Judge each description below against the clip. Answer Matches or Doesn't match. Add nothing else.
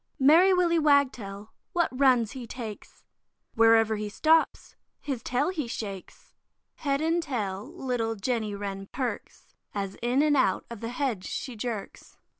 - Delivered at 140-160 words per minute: Matches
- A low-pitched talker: Doesn't match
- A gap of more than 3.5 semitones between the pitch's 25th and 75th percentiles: Matches